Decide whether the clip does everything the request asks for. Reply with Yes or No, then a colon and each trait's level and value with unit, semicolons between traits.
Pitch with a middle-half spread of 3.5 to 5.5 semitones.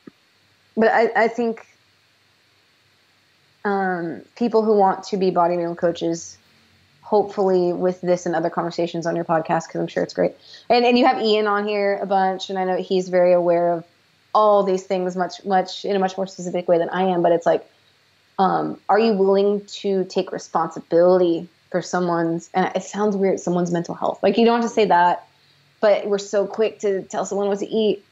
No: average, 2.9 semitones